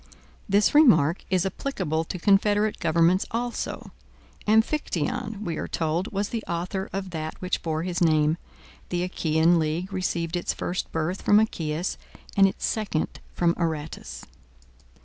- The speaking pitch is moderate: Yes, medium, 175 Hz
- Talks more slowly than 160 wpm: Yes, average, 140 wpm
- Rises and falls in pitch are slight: No, average, 3.6 semitones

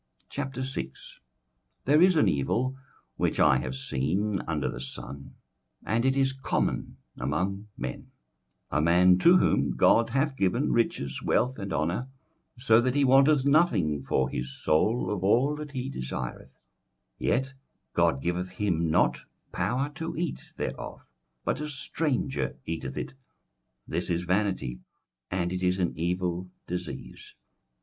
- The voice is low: Yes, low, 100 Hz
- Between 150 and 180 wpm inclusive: No, average, 140 wpm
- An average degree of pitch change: No, wide, 8.2 semitones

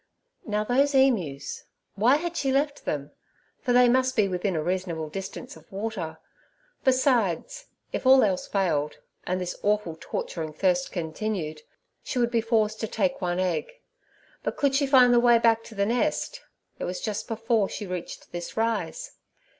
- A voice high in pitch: Yes, high, 215 Hz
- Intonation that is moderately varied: No, wide, 5.8 semitones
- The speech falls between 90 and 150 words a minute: No, average, 165 wpm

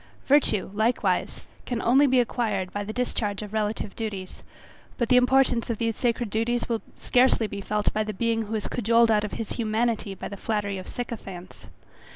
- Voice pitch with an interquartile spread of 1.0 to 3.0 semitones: Yes, narrow, 2.4 semitones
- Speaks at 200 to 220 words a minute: No, average, 190 wpm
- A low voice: No, high, 225 Hz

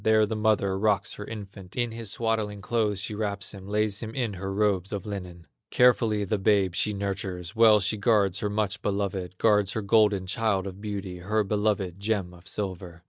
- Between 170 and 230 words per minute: Yes, average, 195 wpm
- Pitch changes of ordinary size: No, narrow, 1.9 semitones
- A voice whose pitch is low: Yes, low, 100 Hz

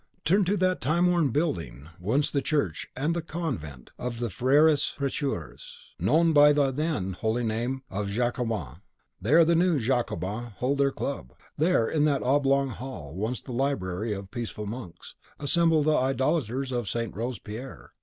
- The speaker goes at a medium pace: Yes, average, 165 wpm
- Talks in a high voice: No, low, 130 Hz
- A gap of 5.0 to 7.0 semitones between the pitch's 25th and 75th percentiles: Yes, wide, 5.4 semitones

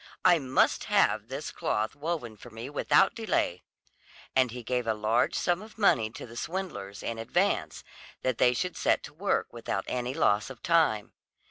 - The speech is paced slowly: No, average, 175 wpm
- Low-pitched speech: Yes, low, 125 Hz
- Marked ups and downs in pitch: Yes, wide, 7.1 semitones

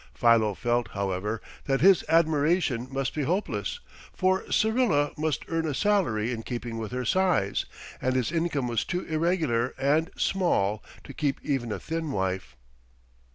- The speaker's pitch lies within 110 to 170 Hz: Yes, low, 135 Hz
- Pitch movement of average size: No, wide, 6.2 semitones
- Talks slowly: No, average, 155 wpm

